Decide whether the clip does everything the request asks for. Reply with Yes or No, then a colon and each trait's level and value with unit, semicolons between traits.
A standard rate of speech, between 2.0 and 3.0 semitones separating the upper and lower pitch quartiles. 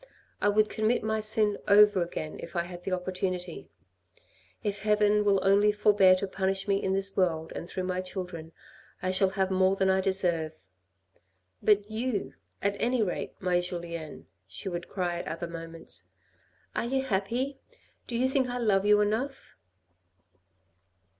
Yes: average, 160 wpm; average, 2.7 semitones